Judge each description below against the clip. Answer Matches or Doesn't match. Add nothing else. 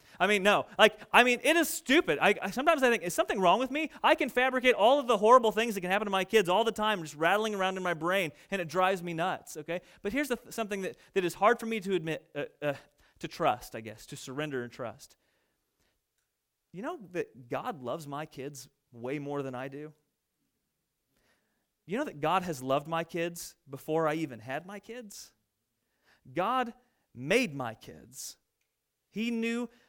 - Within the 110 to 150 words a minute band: Doesn't match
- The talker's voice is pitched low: Doesn't match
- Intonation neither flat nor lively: Doesn't match